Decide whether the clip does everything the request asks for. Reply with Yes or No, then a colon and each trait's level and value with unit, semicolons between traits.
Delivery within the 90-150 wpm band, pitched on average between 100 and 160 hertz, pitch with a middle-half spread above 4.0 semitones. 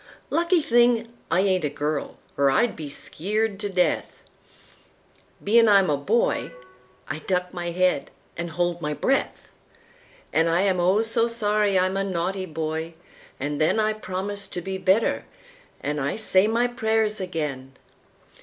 No: average, 145 wpm; medium, 185 Hz; average, 4.8 semitones